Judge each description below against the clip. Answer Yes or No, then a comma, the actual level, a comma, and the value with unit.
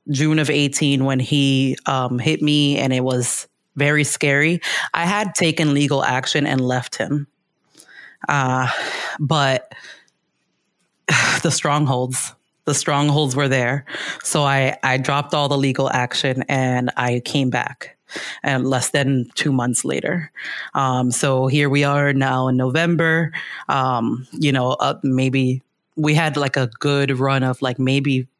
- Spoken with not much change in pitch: Yes, narrow, 2.3 semitones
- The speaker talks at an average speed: Yes, average, 145 wpm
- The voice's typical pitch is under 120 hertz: No, medium, 140 Hz